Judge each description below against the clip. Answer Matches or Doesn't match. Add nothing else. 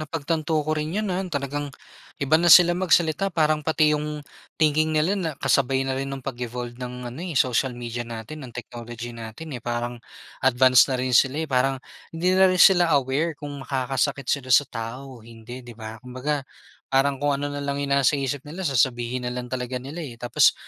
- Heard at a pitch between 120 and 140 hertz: Matches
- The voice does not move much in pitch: Doesn't match